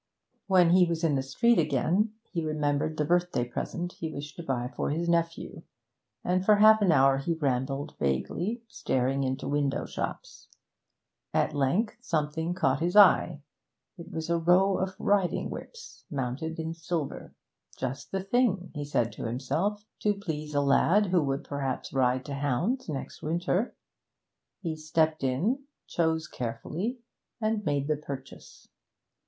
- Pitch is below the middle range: No, medium, 160 Hz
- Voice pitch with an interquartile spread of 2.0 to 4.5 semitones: No, average, 4.9 semitones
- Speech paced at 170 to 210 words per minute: No, average, 155 wpm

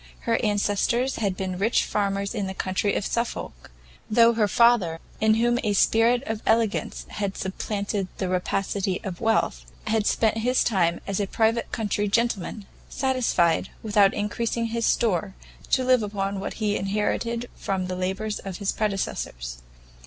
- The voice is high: Yes, high, 210 Hz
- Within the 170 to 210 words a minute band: No, average, 155 wpm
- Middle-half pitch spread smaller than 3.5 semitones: Yes, average, 2.9 semitones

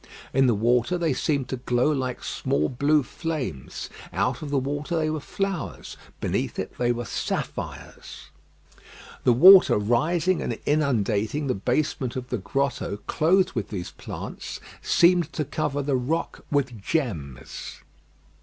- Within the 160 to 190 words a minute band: No, average, 145 wpm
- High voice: No, low, 135 Hz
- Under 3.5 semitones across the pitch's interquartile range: No, average, 4.4 semitones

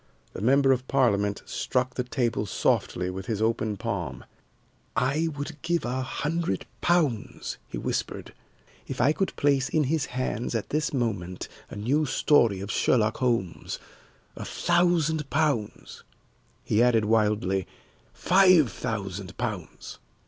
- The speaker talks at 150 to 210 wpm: No, slow, 135 wpm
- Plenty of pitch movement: Yes, wide, 5.9 semitones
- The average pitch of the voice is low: Yes, low, 125 Hz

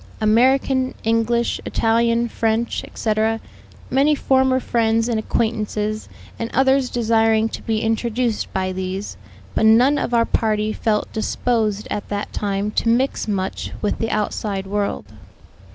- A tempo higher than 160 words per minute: No, slow, 135 wpm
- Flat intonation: Yes, narrow, 1.9 semitones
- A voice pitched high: Yes, high, 225 Hz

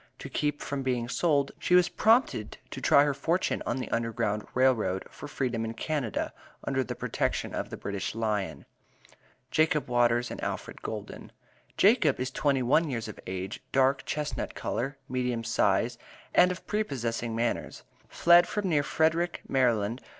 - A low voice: Yes, low, 130 Hz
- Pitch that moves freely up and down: No, average, 4.6 semitones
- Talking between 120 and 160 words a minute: Yes, average, 155 wpm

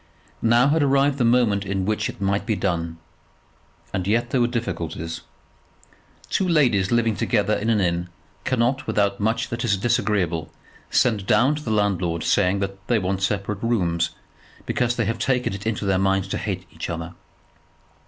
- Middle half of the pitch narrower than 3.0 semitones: No, average, 3.7 semitones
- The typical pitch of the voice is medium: No, low, 105 Hz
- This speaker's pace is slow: No, average, 175 wpm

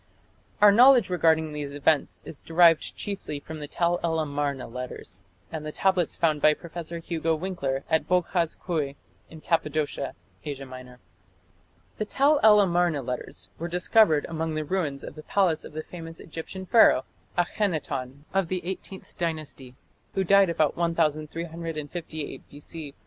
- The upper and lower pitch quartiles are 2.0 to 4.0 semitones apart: Yes, average, 3.1 semitones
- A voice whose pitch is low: No, medium, 160 Hz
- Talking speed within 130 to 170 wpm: Yes, average, 150 wpm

